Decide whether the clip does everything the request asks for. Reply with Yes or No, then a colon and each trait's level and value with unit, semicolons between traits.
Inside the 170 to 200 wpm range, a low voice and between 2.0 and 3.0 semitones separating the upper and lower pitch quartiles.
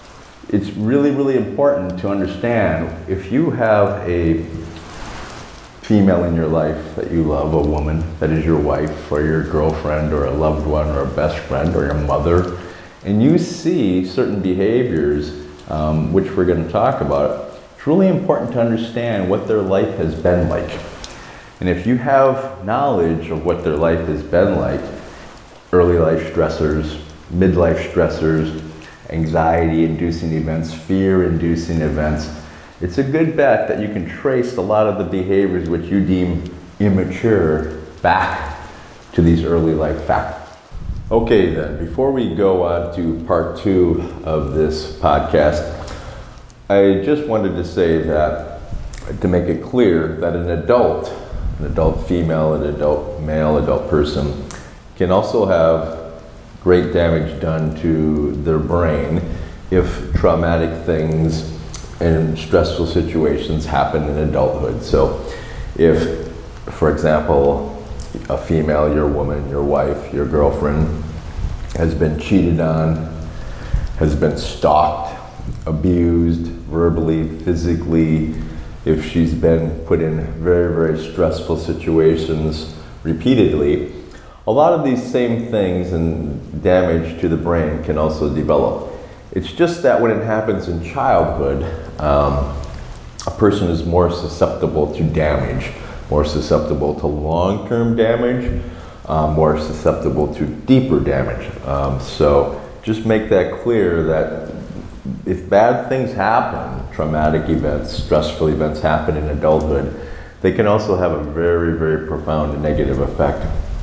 No: slow, 135 wpm; very low, 80 Hz; narrow, 2.6 semitones